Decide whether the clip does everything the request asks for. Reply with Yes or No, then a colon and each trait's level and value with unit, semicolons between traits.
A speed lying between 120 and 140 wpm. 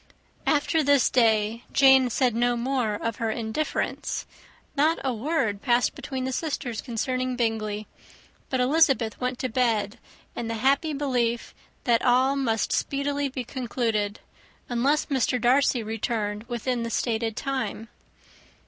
Yes: slow, 135 wpm